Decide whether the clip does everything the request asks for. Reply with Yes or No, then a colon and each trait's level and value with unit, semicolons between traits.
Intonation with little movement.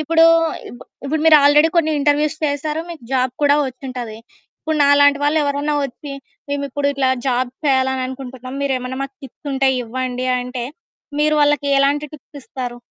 Yes: narrow, 2.3 semitones